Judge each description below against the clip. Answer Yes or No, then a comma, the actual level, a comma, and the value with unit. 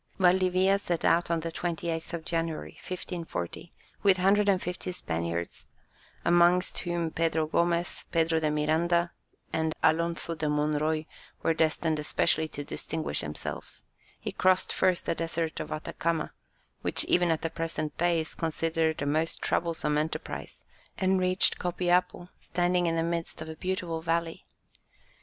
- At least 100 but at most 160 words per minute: Yes, average, 140 wpm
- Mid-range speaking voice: Yes, medium, 165 Hz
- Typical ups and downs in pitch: No, narrow, 1.8 semitones